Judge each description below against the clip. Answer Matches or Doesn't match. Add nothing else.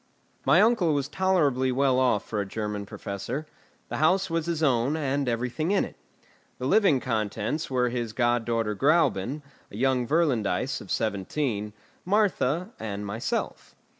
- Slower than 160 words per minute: Matches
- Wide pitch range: Matches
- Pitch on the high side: Doesn't match